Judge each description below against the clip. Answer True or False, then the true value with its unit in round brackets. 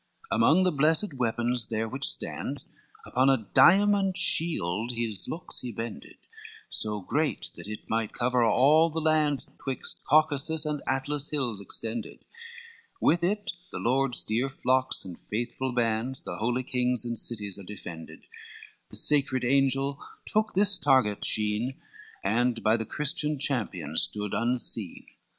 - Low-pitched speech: True (125 Hz)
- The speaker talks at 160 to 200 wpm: False (145 wpm)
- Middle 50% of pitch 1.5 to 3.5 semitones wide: False (4.8 semitones)